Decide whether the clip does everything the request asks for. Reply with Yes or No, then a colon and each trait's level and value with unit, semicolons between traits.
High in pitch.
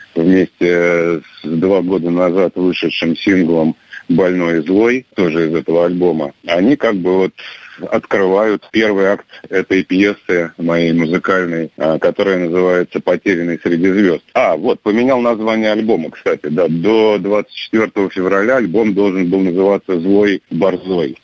No: very low, 95 Hz